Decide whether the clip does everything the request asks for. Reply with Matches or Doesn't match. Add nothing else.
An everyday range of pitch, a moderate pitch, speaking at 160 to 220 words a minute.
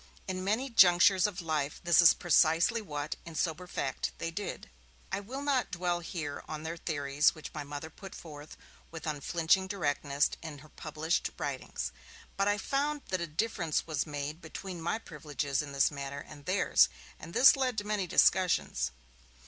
Matches